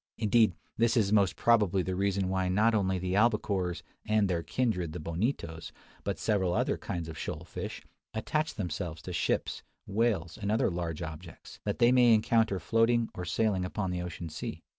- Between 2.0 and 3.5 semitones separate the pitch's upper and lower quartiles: No, average, 4.0 semitones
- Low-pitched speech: Yes, very low, 95 Hz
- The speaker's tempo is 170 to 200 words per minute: Yes, average, 180 wpm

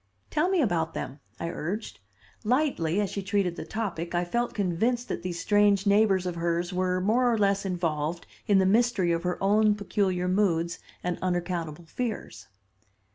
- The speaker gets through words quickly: No, average, 170 wpm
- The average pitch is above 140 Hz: Yes, medium, 185 Hz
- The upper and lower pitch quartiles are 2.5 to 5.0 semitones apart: Yes, average, 3.4 semitones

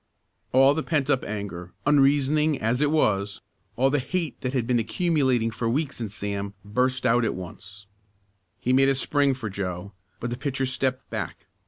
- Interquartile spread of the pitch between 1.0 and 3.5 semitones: No, average, 4.7 semitones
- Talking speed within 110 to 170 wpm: No, average, 180 wpm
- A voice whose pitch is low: Yes, low, 125 Hz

